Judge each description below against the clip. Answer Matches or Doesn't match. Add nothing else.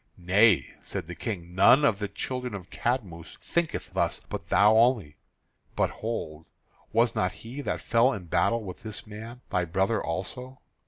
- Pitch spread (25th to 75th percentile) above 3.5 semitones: Matches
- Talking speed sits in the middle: Matches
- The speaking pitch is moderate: Doesn't match